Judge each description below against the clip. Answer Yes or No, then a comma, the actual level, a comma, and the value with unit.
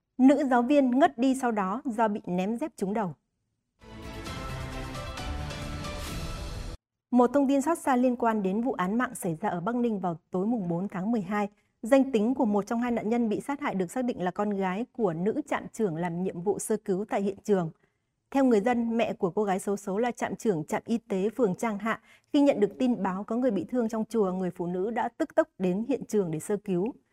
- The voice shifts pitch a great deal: No, average, 4.6 semitones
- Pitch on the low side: No, high, 215 Hz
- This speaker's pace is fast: No, average, 235 wpm